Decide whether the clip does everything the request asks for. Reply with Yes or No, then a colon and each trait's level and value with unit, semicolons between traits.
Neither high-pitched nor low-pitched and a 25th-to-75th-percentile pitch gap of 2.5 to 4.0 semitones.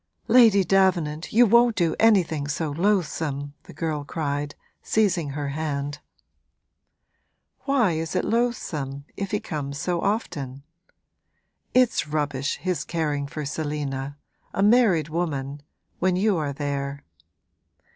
No: medium, 155 Hz; average, 5.2 semitones